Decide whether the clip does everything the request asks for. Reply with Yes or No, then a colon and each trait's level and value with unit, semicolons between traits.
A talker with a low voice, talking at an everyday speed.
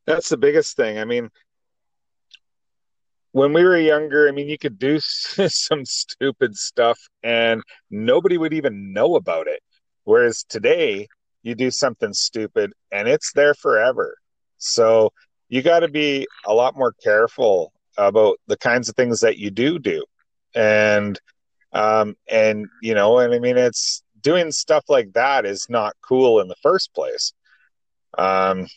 No: medium, 145 Hz; average, 155 wpm